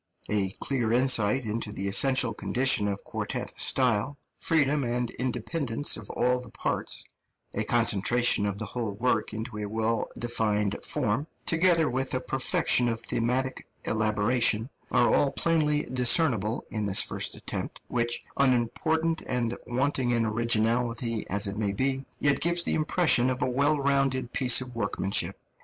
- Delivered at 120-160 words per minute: Yes, average, 150 wpm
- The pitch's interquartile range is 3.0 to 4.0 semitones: Yes, average, 3.4 semitones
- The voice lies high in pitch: No, low, 120 Hz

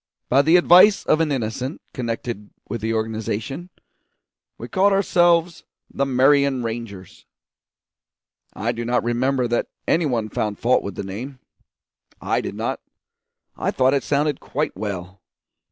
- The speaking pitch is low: Yes, low, 125 Hz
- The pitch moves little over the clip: No, average, 4.6 semitones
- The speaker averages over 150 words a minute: No, average, 140 wpm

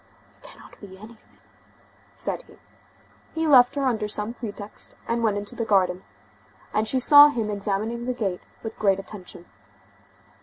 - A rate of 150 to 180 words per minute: Yes, average, 155 wpm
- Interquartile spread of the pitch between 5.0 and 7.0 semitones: No, average, 3.1 semitones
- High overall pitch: Yes, high, 215 Hz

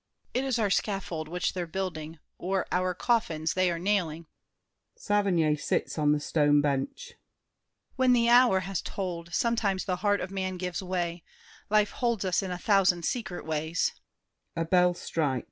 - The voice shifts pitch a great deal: No, average, 3.5 semitones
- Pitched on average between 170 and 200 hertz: Yes, medium, 185 Hz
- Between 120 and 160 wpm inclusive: Yes, average, 150 wpm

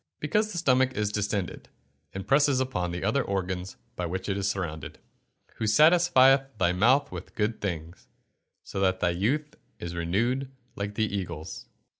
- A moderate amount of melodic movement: No, wide, 6.4 semitones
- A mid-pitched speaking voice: No, low, 105 Hz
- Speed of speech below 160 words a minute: No, average, 170 wpm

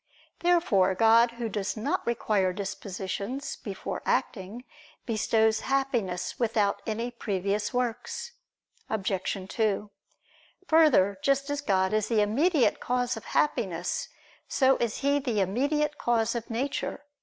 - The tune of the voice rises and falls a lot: No, average, 4.8 semitones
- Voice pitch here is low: No, high, 225 Hz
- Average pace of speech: No, slow, 120 wpm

